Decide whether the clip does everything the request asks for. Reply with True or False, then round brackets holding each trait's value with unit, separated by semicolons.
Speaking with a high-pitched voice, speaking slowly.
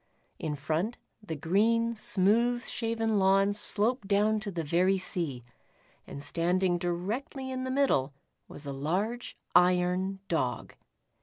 True (195 Hz; 130 wpm)